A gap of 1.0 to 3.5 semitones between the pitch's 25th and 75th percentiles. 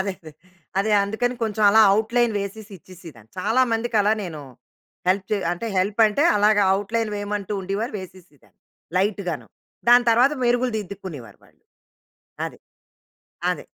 Yes: average, 3.1 semitones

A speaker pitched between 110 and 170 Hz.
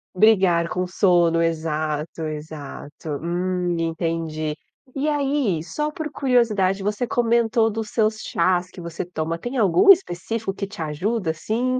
No: medium, 185 Hz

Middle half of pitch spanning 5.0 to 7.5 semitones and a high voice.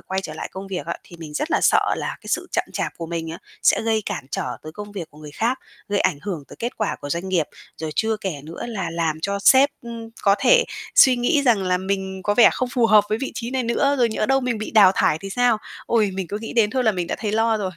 No: average, 4.5 semitones; high, 210 Hz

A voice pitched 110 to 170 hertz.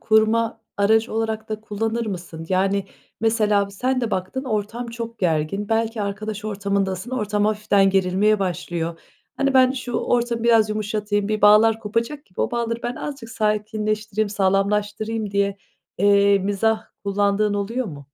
No: high, 215 Hz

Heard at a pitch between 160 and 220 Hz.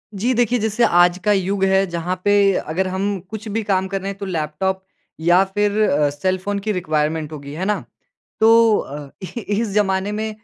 Yes: high, 190 Hz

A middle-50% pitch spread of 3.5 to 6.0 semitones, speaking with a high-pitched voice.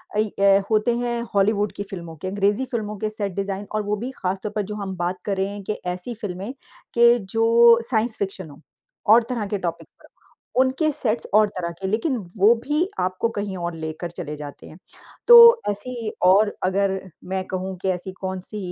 No: average, 2.9 semitones; high, 200 Hz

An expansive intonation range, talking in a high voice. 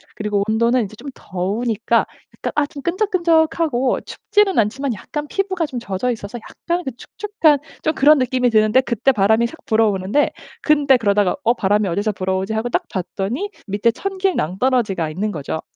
Yes: wide, 6.3 semitones; high, 235 Hz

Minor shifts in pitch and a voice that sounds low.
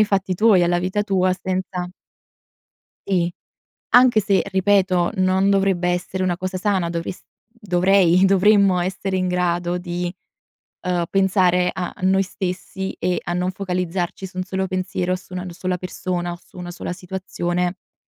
No: narrow, 1.3 semitones; medium, 185 Hz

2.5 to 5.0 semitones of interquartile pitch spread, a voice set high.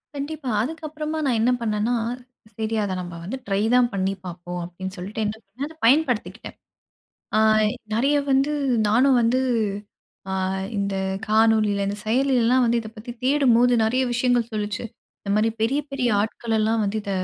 Yes: average, 3.9 semitones; high, 225 Hz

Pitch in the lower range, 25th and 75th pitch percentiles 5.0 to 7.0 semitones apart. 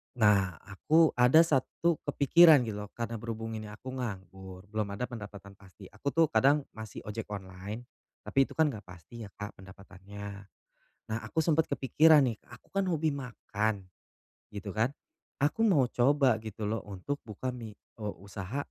Yes: low, 110 Hz; wide, 5.6 semitones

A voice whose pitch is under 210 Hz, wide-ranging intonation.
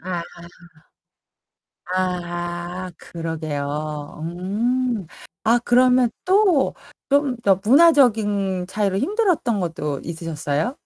Yes: high, 190 Hz; wide, 6.7 semitones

